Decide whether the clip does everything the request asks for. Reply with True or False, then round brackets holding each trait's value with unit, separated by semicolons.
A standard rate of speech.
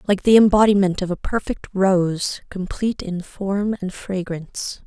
True (150 wpm)